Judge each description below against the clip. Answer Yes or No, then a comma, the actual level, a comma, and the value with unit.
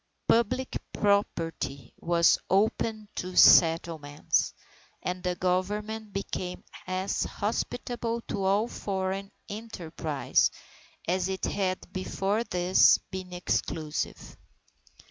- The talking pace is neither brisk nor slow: No, slow, 90 wpm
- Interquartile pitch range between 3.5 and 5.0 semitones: No, average, 2.7 semitones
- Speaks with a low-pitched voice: No, high, 190 Hz